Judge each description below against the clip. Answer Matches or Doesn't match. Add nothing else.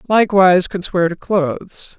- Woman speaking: Matches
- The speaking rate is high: Doesn't match